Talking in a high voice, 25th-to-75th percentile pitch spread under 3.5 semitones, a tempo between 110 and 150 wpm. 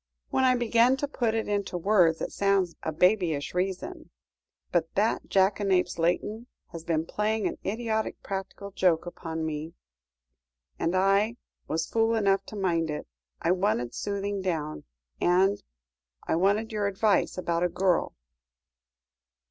No: high, 195 Hz; average, 3.9 semitones; average, 140 wpm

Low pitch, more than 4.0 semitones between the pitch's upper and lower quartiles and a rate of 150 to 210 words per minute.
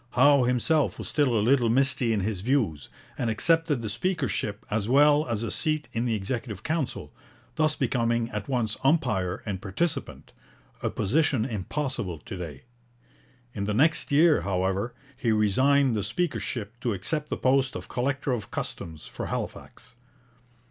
Yes: low, 120 Hz; average, 5.3 semitones; average, 155 wpm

